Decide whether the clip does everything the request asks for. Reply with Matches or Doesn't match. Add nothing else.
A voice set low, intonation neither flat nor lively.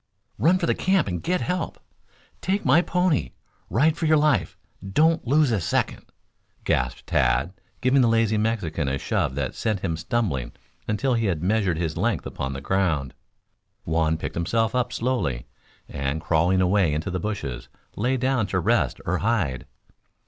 Doesn't match